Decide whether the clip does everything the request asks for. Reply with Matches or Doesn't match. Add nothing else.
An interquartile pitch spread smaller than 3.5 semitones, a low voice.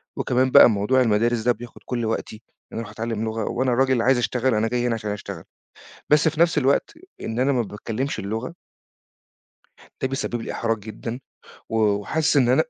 Matches